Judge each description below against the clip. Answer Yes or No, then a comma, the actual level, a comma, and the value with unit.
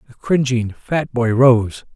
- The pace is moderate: Yes, average, 155 wpm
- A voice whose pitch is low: Yes, low, 120 Hz